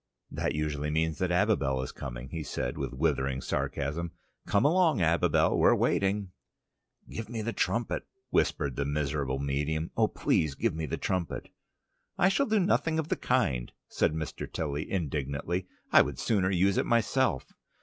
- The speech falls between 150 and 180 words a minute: Yes, average, 160 wpm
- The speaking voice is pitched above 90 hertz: No, very low, 80 Hz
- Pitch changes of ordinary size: No, wide, 6.2 semitones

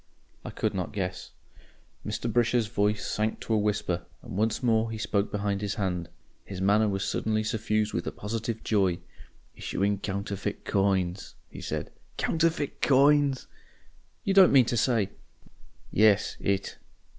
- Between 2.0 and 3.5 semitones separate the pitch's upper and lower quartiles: Yes, narrow, 2.5 semitones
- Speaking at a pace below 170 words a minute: Yes, average, 150 wpm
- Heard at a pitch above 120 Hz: No, low, 105 Hz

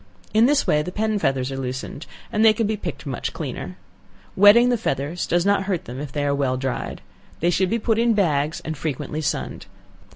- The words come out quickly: Yes, fast, 215 wpm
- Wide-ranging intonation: Yes, wide, 7.2 semitones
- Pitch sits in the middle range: Yes, medium, 175 Hz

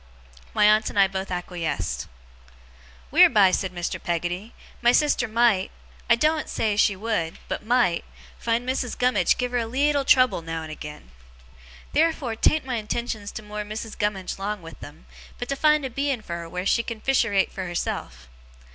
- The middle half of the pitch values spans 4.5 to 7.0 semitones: Yes, average, 5.2 semitones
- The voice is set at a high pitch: Yes, high, 215 Hz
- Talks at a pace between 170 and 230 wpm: Yes, average, 175 wpm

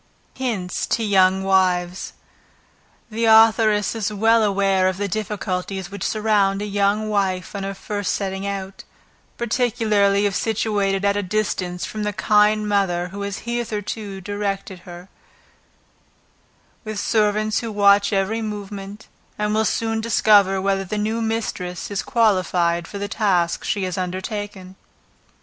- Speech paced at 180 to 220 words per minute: No, average, 140 wpm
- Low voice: No, high, 200 Hz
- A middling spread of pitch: No, narrow, 1.9 semitones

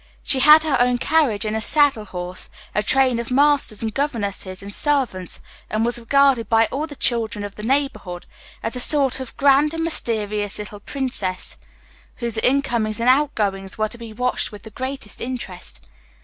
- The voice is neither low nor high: No, high, 235 Hz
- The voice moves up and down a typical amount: Yes, average, 4.6 semitones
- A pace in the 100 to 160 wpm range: No, average, 180 wpm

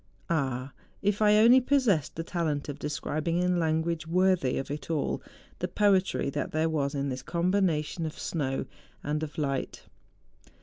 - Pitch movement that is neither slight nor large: Yes, average, 4.0 semitones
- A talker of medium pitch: Yes, medium, 160 Hz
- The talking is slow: No, average, 160 wpm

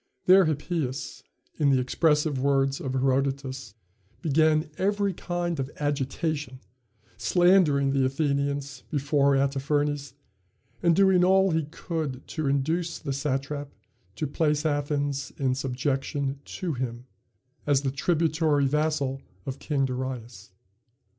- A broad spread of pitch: No, average, 2.7 semitones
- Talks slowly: Yes, slow, 115 wpm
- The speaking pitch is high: No, medium, 140 Hz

